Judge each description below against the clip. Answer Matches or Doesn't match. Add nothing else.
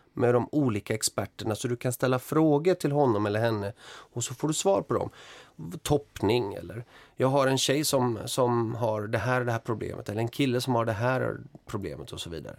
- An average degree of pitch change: Matches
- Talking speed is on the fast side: Matches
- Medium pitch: Doesn't match